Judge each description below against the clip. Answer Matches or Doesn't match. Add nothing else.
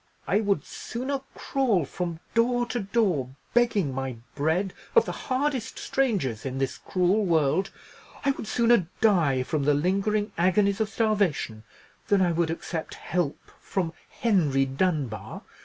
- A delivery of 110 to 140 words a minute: Matches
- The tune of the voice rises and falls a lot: Matches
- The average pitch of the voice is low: Doesn't match